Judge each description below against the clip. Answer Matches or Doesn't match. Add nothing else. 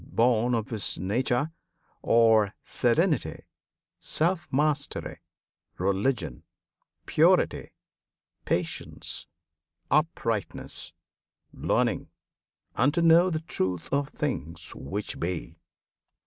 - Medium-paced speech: Doesn't match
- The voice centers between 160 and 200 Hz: Doesn't match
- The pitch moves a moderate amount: Doesn't match